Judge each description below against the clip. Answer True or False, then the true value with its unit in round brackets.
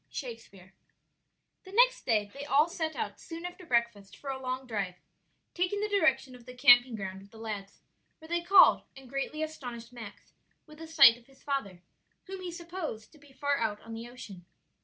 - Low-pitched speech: False (260 Hz)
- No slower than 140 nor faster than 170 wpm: False (195 wpm)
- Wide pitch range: True (6.1 semitones)